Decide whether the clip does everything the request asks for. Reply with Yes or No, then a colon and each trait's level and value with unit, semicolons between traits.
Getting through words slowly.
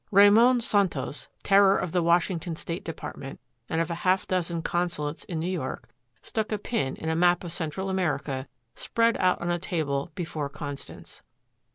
No: average, 170 wpm